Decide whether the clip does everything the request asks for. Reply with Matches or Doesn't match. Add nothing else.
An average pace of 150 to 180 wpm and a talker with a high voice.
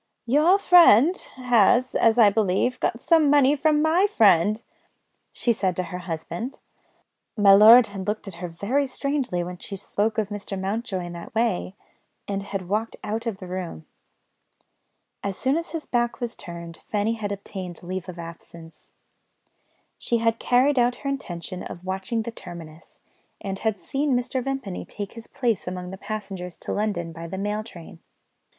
Matches